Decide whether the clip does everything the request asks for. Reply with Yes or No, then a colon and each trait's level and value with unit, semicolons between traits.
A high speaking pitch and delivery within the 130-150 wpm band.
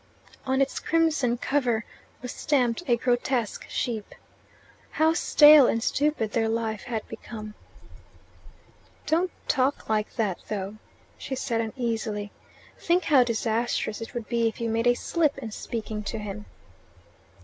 Yes: high, 235 Hz; average, 140 wpm